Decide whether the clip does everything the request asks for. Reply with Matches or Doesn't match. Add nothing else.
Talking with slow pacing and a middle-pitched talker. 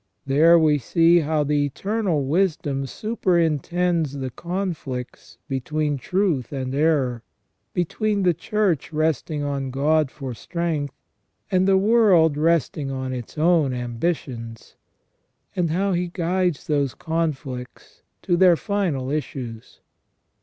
Matches